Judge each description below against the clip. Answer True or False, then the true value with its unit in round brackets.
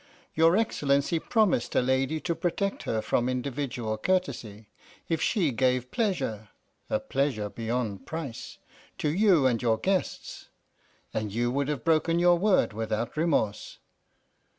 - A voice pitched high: False (140 Hz)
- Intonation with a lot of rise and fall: True (6.4 semitones)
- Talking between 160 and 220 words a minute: False (135 wpm)